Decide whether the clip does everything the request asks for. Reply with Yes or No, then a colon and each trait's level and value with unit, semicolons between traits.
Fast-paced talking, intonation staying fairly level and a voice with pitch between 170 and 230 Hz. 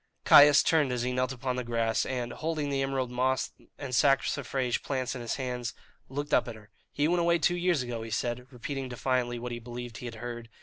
No: fast, 220 wpm; narrow, 2.3 semitones; low, 125 Hz